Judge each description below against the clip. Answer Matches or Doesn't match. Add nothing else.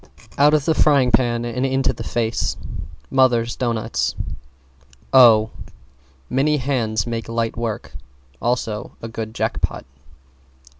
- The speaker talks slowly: Matches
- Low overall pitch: Matches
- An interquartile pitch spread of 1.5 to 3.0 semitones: Matches